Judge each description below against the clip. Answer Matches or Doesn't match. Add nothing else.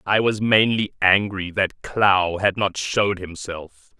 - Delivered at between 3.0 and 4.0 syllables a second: Matches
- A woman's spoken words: Doesn't match